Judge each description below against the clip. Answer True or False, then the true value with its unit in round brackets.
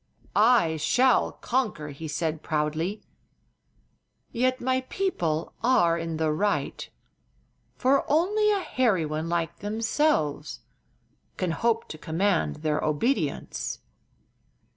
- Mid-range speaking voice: True (175 Hz)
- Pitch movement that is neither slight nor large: False (8.3 semitones)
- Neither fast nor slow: False (105 wpm)